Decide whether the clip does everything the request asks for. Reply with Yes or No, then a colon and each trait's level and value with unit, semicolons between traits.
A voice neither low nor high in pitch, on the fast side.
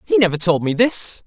Yes: medium, 175 Hz; fast, 235 wpm